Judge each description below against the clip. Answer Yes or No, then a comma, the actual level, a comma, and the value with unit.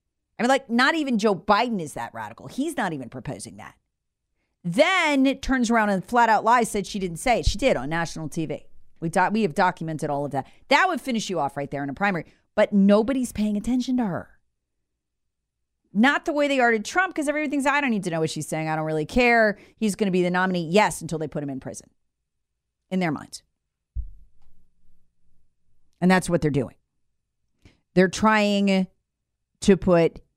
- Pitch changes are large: Yes, wide, 7.5 semitones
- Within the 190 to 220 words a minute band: Yes, fast, 205 wpm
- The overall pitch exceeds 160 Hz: Yes, medium, 185 Hz